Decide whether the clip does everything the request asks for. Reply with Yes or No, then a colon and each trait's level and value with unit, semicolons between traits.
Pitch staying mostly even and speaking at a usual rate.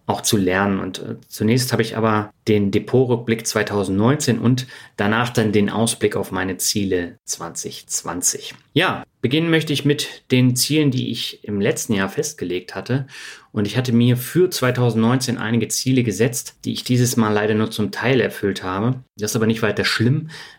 No: average, 3.2 semitones; average, 170 wpm